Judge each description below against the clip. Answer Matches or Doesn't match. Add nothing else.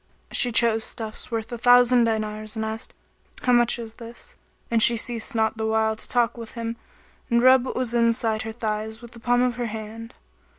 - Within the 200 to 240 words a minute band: Matches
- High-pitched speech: Matches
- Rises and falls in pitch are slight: Matches